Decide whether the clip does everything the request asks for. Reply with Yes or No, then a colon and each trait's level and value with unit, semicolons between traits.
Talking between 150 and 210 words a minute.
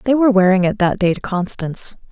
No: fast, 225 wpm